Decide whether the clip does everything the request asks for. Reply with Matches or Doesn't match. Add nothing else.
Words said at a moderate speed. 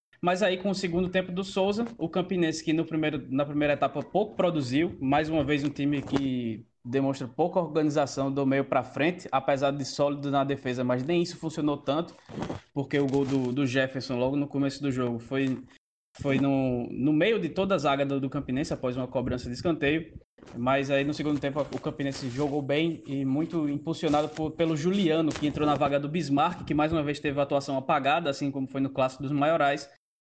Doesn't match